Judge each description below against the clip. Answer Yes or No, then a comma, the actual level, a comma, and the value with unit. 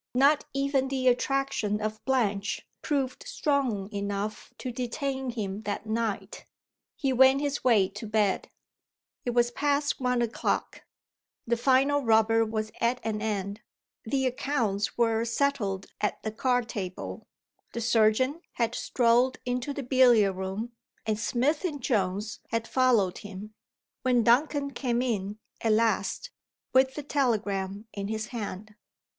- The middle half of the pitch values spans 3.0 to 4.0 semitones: Yes, average, 3.7 semitones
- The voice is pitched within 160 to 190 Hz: No, high, 235 Hz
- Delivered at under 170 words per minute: Yes, average, 140 wpm